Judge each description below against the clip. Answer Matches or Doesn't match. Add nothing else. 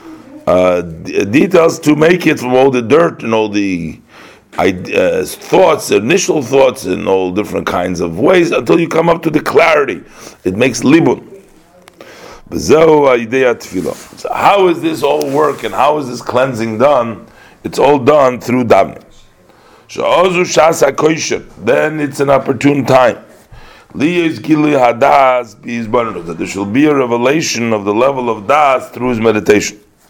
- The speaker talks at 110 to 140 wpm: Matches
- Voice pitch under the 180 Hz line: Matches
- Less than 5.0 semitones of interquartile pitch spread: Doesn't match